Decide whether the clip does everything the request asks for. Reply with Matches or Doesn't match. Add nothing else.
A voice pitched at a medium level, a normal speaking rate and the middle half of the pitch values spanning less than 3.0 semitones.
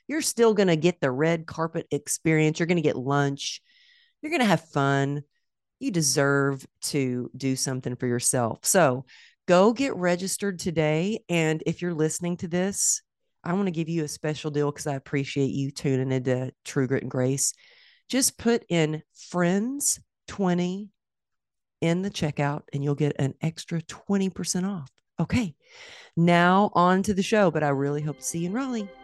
Doesn't match